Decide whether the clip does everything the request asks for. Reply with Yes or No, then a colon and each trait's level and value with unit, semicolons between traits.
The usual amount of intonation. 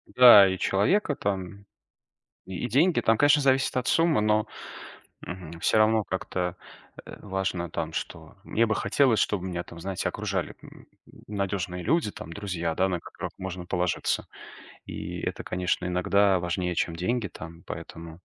Yes: average, 3.5 semitones